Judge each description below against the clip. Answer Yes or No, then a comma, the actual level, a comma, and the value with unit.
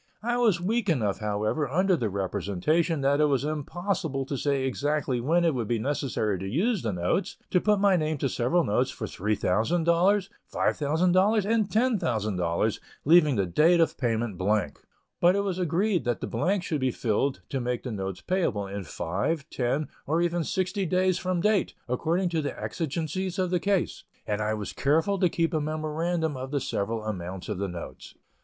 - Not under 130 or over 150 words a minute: No, average, 185 wpm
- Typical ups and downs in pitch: No, wide, 7.9 semitones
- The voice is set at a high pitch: No, medium, 150 Hz